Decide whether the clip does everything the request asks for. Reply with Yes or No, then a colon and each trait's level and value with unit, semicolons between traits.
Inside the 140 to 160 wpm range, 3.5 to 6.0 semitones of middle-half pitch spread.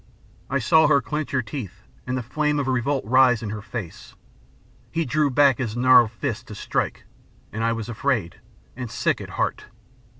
No: average, 180 wpm; average, 3.8 semitones